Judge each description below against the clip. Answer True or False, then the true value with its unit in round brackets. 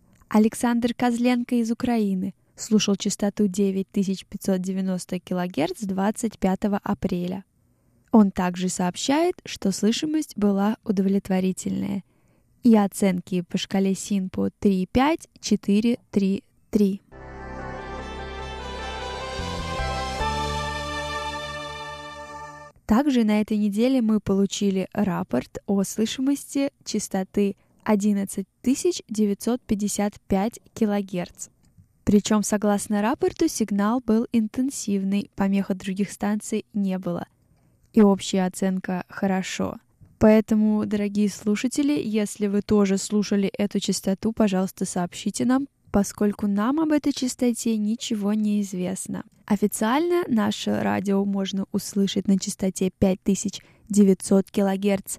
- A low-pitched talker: False (205 Hz)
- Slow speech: True (90 wpm)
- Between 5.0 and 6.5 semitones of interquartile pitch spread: False (2.4 semitones)